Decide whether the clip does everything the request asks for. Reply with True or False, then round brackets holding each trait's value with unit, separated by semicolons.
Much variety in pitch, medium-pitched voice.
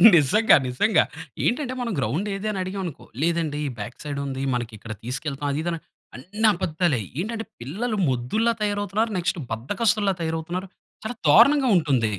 True (7.5 semitones; 175 Hz)